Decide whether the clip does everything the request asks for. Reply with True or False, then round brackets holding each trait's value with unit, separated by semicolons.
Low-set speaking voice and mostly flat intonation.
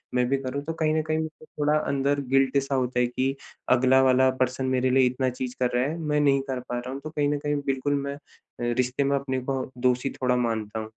True (130 Hz; 2.0 semitones)